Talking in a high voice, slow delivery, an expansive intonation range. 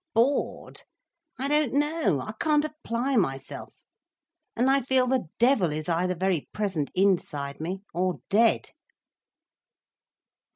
Yes: high, 215 Hz; slow, 120 wpm; wide, 7.4 semitones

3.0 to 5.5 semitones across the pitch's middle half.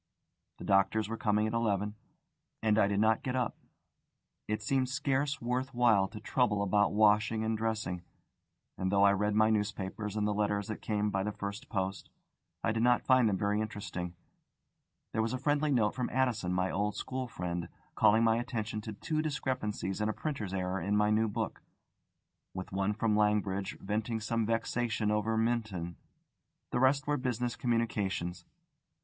No: narrow, 2.5 semitones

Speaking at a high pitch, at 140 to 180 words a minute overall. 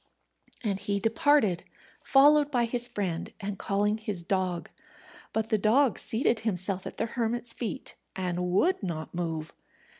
Yes: high, 210 Hz; average, 145 wpm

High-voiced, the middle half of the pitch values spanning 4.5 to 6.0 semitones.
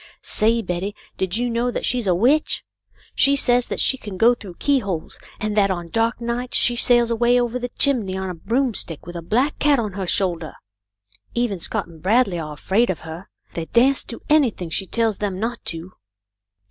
Yes: high, 220 Hz; average, 4.8 semitones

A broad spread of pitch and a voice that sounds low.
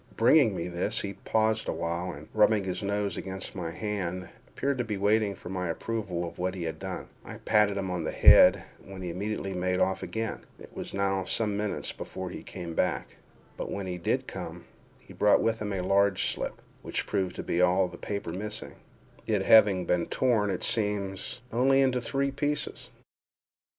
No: average, 2.8 semitones; low, 100 Hz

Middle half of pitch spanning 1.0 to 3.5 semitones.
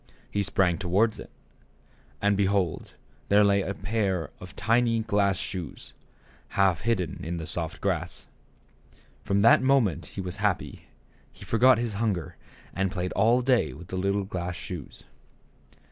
Yes: average, 3.2 semitones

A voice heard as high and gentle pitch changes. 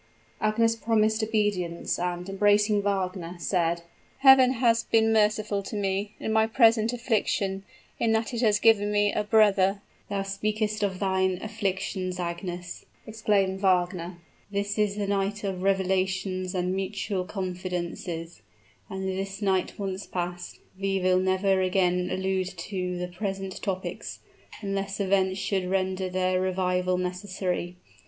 Yes: high, 195 Hz; narrow, 2.1 semitones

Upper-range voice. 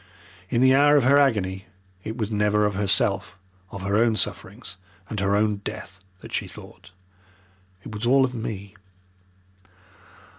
No: low, 105 Hz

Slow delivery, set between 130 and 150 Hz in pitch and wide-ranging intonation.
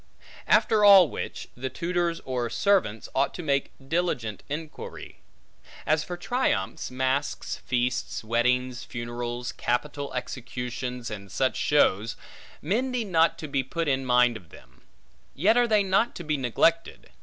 No: average, 145 wpm; low, 135 Hz; wide, 5.8 semitones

